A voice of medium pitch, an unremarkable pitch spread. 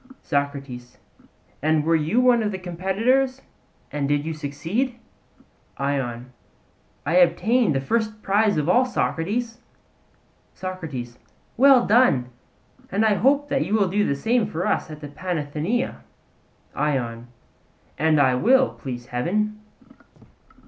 No: medium, 175 Hz; wide, 7.7 semitones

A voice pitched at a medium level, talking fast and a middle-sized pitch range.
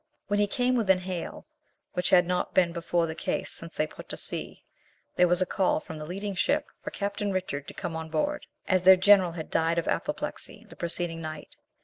Yes: medium, 180 Hz; fast, 215 wpm; average, 3.1 semitones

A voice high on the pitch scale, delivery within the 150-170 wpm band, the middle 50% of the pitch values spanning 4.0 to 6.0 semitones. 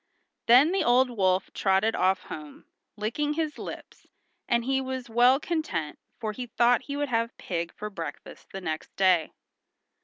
Yes: high, 230 Hz; average, 160 wpm; wide, 5.6 semitones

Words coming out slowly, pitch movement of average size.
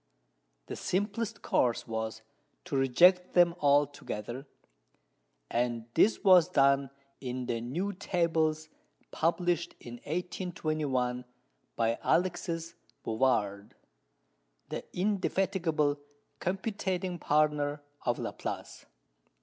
No: slow, 85 wpm; wide, 6.1 semitones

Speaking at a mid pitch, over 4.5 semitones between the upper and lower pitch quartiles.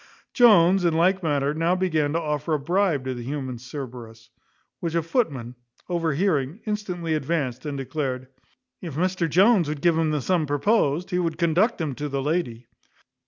No: medium, 160 Hz; average, 4.2 semitones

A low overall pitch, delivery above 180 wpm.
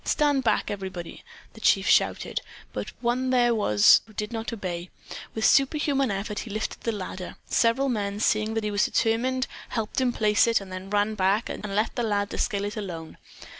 No: high, 215 Hz; average, 190 wpm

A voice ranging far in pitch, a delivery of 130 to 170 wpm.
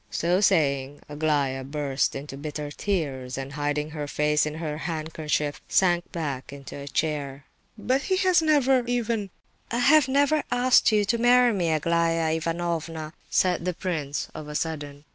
Yes: wide, 5.7 semitones; average, 160 wpm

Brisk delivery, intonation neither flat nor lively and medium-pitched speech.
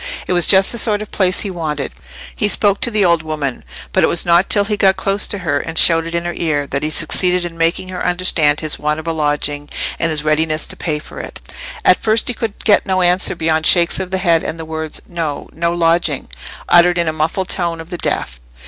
Yes: fast, 240 wpm; average, 3.0 semitones; medium, 170 Hz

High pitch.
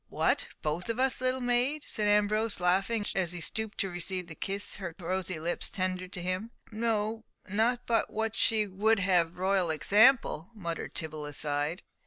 Yes: high, 195 Hz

